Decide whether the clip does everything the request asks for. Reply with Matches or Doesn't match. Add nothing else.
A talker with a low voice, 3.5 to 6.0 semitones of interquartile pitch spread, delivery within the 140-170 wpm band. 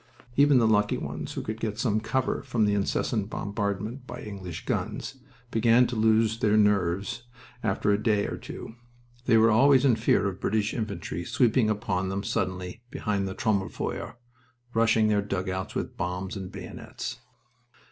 Doesn't match